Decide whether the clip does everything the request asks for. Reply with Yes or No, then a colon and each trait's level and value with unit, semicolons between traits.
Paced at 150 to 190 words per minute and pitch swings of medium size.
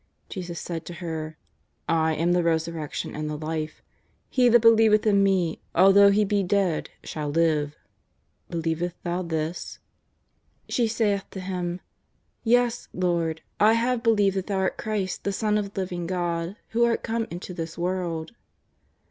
Yes: average, 160 wpm; average, 3.7 semitones